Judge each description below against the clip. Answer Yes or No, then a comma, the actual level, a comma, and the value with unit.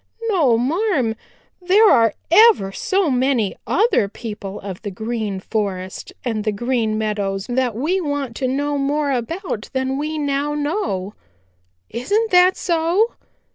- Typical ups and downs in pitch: No, wide, 7.4 semitones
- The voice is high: Yes, very high, 265 Hz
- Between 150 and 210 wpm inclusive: No, slow, 135 wpm